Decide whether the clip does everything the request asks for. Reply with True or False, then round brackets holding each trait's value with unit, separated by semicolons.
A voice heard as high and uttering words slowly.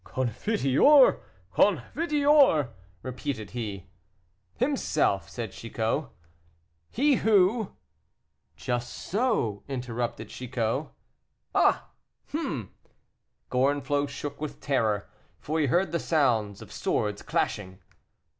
False (135 Hz; 90 wpm)